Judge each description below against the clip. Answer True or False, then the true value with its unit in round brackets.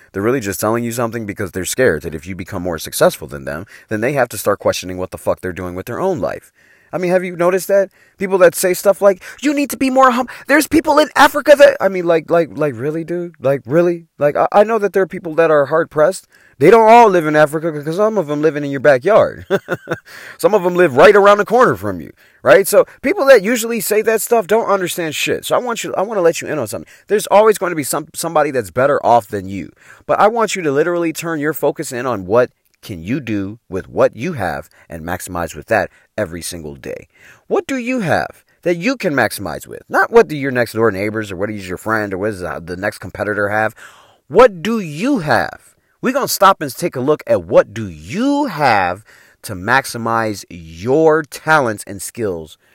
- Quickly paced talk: True (240 wpm)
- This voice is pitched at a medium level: True (155 Hz)